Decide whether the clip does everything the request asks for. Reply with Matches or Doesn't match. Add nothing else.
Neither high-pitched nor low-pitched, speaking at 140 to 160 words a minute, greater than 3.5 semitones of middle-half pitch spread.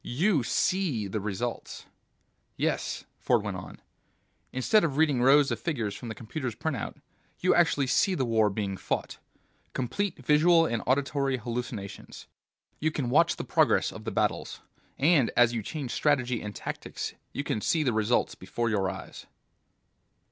Doesn't match